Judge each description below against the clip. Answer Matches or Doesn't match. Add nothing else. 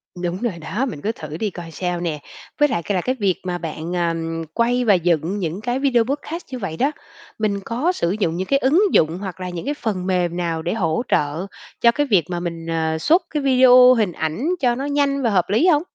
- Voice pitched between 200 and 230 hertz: Doesn't match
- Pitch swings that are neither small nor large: Doesn't match